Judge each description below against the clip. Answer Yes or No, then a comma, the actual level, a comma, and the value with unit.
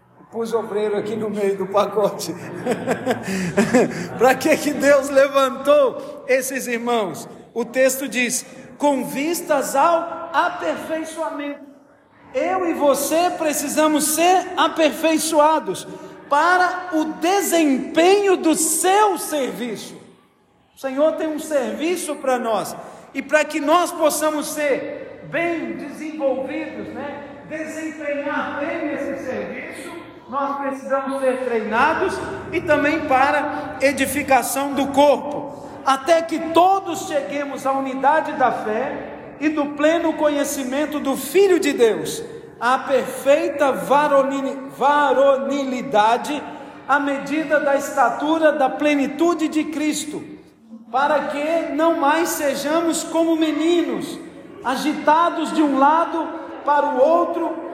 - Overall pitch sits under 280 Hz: No, very high, 290 Hz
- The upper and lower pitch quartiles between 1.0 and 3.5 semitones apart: Yes, average, 2.9 semitones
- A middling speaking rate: No, slow, 110 wpm